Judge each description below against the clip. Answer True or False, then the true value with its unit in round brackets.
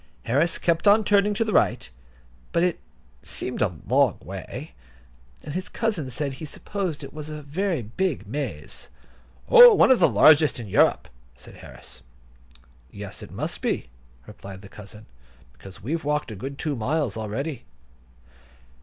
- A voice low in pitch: False (150 Hz)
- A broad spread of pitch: True (7.7 semitones)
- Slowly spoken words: False (155 wpm)